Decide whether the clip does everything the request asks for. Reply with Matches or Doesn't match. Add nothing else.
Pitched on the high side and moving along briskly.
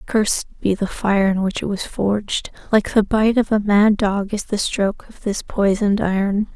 Matches